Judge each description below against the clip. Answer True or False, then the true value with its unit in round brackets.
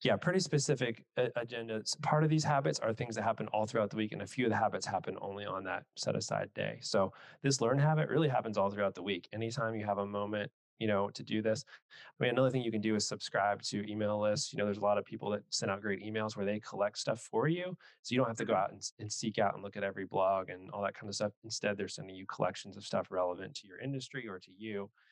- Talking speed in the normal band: False (275 wpm)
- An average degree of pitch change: True (3.5 semitones)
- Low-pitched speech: True (110 Hz)